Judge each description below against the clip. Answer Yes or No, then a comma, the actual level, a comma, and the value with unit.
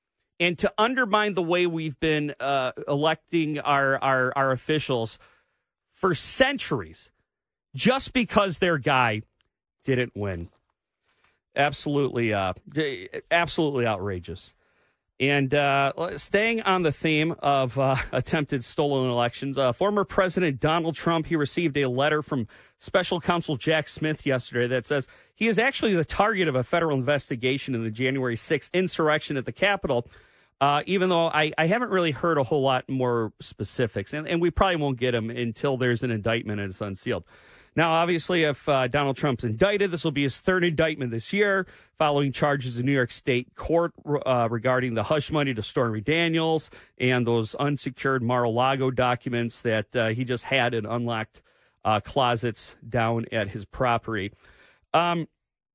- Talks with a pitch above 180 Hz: No, medium, 140 Hz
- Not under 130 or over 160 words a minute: Yes, average, 155 wpm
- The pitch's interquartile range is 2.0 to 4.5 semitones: No, average, 5.1 semitones